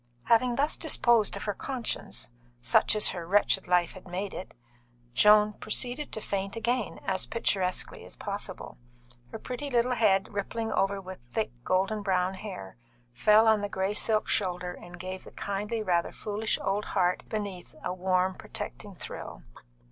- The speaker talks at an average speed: Yes, average, 160 wpm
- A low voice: No, high, 200 Hz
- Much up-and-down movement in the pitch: No, average, 2.9 semitones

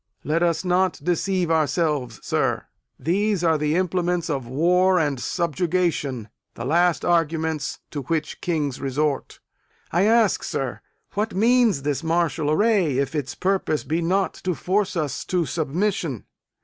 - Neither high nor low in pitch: Yes, medium, 165 Hz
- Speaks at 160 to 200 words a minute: No, average, 140 wpm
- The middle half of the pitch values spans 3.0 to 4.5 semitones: Yes, average, 3.7 semitones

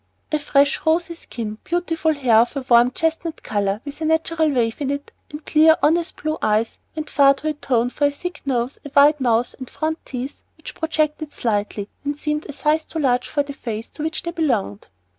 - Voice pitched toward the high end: Yes, very high, 285 Hz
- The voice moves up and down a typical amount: Yes, average, 4.4 semitones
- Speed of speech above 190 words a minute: Yes, fast, 205 wpm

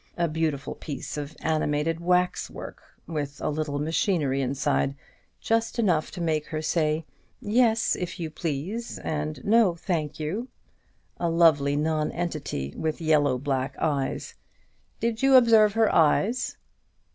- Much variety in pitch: No, average, 3.8 semitones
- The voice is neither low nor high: Yes, medium, 160 Hz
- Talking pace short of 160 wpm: Yes, slow, 135 wpm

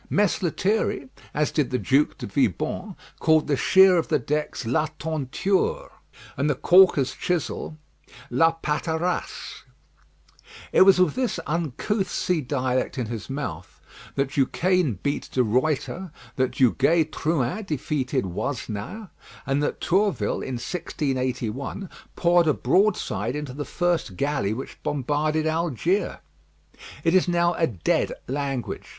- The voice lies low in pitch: No, medium, 150 Hz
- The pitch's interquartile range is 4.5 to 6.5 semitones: Yes, average, 5.2 semitones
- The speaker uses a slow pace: Yes, slow, 130 wpm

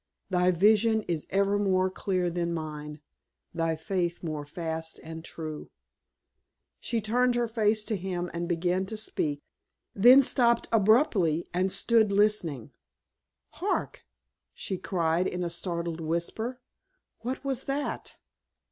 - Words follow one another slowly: Yes, slow, 130 wpm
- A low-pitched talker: No, medium, 185 Hz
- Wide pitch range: No, average, 4.6 semitones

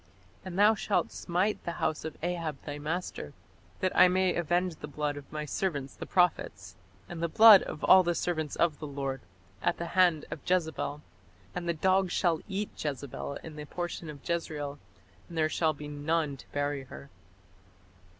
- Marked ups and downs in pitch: No, average, 3.3 semitones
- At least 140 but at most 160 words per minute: No, average, 180 wpm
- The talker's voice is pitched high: No, medium, 160 Hz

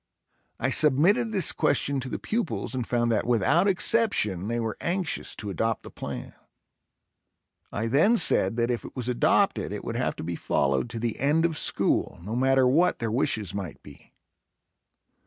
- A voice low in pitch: Yes, low, 125 Hz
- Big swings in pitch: Yes, wide, 6.3 semitones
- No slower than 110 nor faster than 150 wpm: No, average, 175 wpm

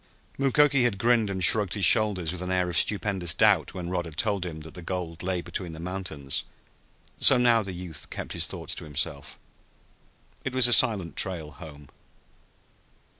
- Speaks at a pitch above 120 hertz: No, very low, 90 Hz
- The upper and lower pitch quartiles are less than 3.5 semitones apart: No, average, 4.3 semitones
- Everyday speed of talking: Yes, average, 180 wpm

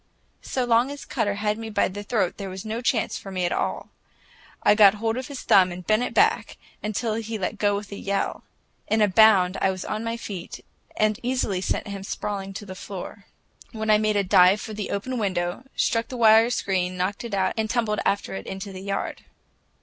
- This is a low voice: No, high, 205 Hz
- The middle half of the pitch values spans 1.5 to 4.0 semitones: Yes, narrow, 2.5 semitones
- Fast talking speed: Yes, fast, 220 wpm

